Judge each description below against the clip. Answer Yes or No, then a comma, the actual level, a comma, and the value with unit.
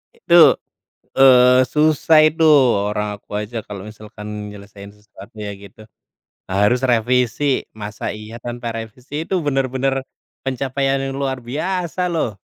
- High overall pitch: No, low, 125 Hz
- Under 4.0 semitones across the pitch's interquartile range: No, average, 4.3 semitones